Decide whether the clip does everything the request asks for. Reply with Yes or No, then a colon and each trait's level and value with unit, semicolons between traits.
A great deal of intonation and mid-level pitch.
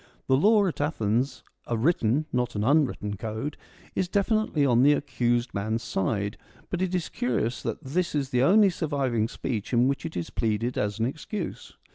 No: wide, 5.8 semitones; low, 130 Hz